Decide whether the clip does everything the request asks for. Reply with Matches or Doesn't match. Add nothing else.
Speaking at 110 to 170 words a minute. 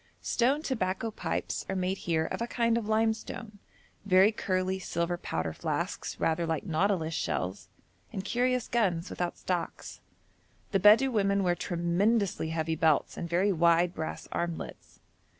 Matches